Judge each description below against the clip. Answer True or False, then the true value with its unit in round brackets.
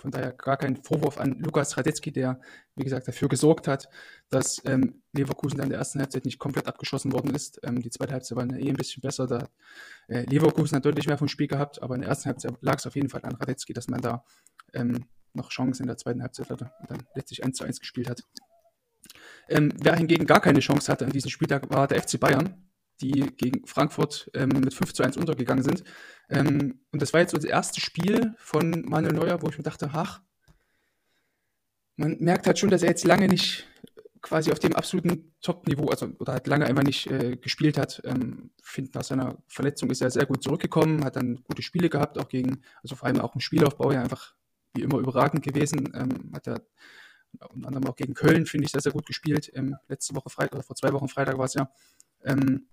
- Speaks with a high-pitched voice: False (140 Hz)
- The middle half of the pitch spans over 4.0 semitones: False (2.8 semitones)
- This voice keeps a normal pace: False (220 wpm)